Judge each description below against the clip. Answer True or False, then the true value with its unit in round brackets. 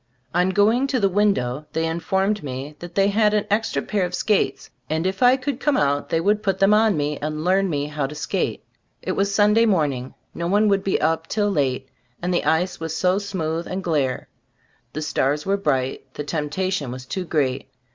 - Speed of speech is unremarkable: False (210 wpm)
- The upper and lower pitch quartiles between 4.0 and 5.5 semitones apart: True (5.2 semitones)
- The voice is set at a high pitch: False (180 Hz)